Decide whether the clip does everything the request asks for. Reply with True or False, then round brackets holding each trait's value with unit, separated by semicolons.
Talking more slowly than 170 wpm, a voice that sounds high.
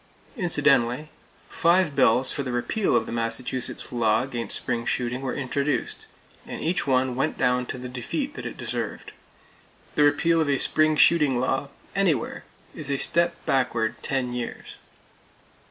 False (155 wpm; 130 Hz)